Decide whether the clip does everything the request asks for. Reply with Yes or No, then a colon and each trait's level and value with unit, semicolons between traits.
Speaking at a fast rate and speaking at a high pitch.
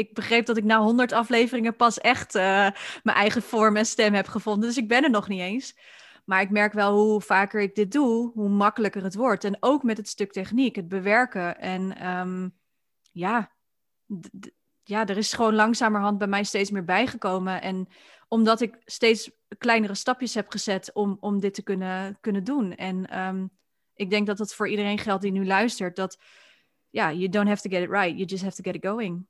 Yes: fast, 215 wpm; high, 210 Hz